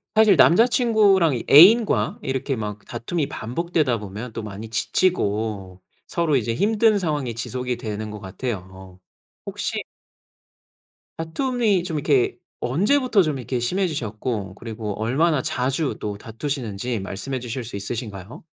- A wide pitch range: Yes, wide, 7.7 semitones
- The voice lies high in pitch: No, low, 125 Hz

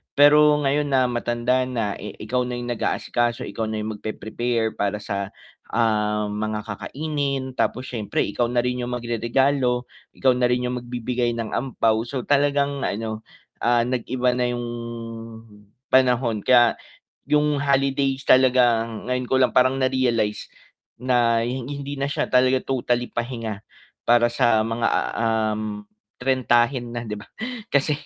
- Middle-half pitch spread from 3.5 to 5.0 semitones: No, narrow, 2.4 semitones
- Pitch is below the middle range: Yes, low, 120 Hz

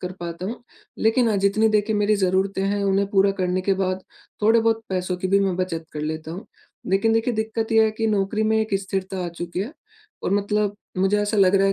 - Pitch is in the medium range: No, high, 195 Hz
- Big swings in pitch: No, narrow, 2.6 semitones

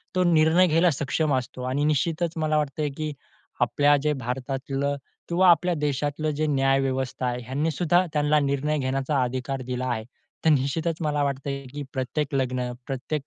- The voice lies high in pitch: No, medium, 145 Hz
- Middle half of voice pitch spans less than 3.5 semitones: Yes, average, 2.7 semitones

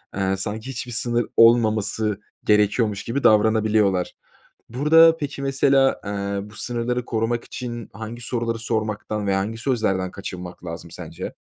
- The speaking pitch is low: Yes, low, 110 Hz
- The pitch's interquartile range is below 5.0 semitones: Yes, average, 2.8 semitones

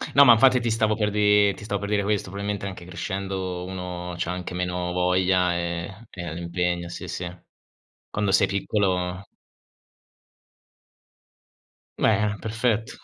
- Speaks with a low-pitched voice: Yes, very low, 95 Hz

